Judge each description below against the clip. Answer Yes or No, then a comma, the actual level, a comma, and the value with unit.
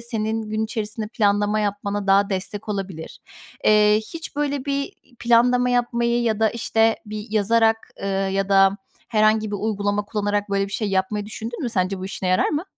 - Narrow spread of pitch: Yes, narrow, 2.3 semitones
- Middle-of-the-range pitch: No, high, 215 Hz